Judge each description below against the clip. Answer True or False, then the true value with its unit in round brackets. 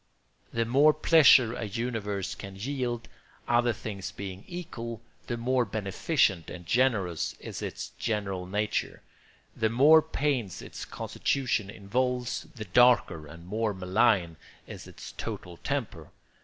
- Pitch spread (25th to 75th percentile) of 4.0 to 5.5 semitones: True (4.4 semitones)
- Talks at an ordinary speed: False (130 wpm)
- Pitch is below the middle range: True (115 Hz)